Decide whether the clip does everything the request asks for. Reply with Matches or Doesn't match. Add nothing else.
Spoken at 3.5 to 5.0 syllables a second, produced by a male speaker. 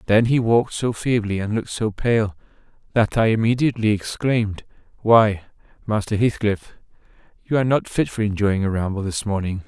Doesn't match